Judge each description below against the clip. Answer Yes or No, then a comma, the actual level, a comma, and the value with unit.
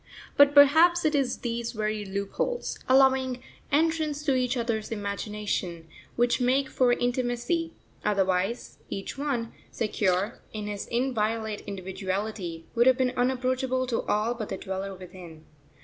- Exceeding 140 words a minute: No, slow, 135 wpm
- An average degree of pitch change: Yes, average, 4.4 semitones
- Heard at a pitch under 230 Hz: No, high, 235 Hz